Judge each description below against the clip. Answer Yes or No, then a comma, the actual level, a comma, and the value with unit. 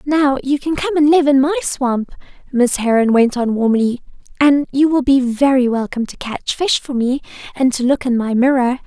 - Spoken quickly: Yes, fast, 210 wpm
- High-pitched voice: Yes, very high, 265 Hz